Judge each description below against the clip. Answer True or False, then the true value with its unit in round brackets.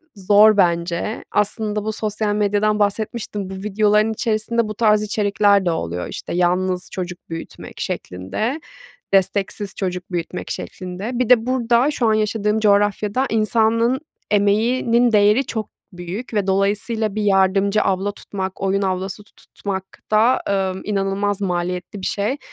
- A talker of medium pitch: False (205 Hz)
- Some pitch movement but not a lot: False (2.3 semitones)